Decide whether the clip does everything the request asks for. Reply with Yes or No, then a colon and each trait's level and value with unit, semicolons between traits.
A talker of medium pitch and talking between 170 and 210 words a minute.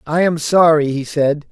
Yes: medium, 155 Hz; average, 200 wpm